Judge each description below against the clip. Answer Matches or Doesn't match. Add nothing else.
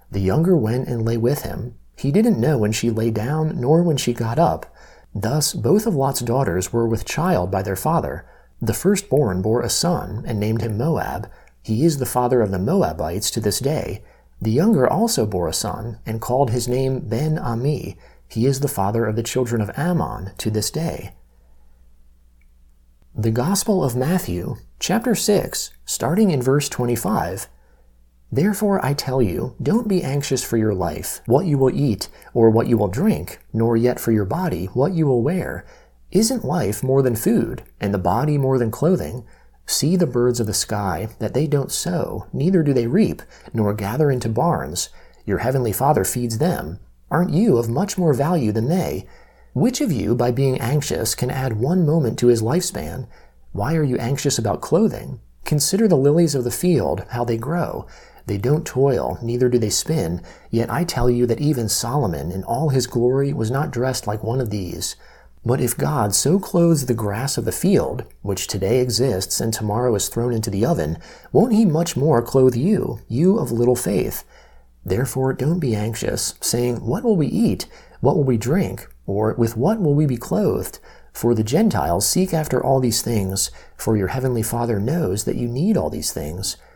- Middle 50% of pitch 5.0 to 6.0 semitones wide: Matches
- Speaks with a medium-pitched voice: Doesn't match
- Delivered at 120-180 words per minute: Doesn't match